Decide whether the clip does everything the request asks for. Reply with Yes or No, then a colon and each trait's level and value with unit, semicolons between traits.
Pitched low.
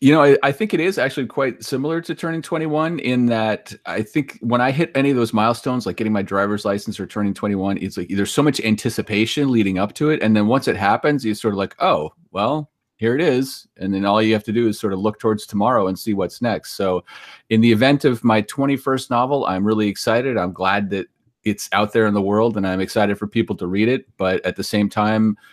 Yes: low, 110 Hz